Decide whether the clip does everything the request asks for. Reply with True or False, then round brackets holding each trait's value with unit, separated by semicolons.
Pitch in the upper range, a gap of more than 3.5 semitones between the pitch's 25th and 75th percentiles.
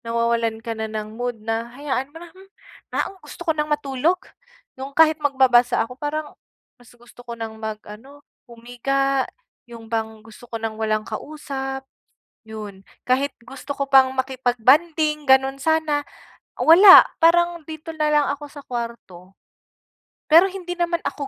True (265 Hz; 4.7 semitones)